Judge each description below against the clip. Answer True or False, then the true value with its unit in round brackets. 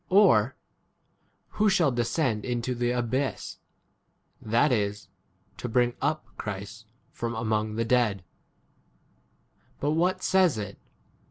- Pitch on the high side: False (120 Hz)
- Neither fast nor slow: False (115 wpm)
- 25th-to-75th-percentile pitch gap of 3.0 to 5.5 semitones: True (4.7 semitones)